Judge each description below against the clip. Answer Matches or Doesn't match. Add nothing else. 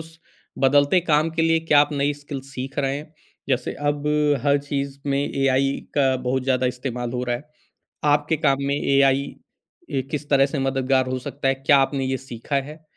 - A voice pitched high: Doesn't match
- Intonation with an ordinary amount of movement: Doesn't match